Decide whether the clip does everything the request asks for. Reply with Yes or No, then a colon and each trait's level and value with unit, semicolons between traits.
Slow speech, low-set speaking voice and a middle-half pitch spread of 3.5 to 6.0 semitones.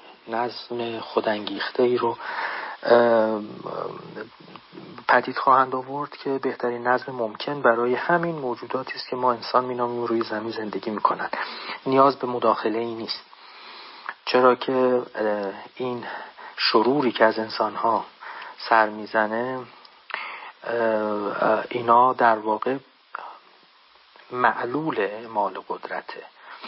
No: slow, 100 wpm; low, 120 Hz; narrow, 2.5 semitones